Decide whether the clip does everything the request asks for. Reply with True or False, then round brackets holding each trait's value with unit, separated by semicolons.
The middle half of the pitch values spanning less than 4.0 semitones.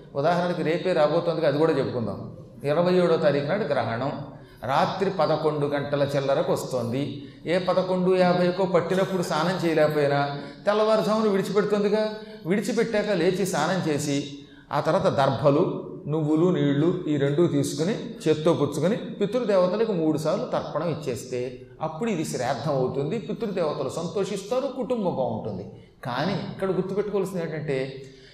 False (5.3 semitones)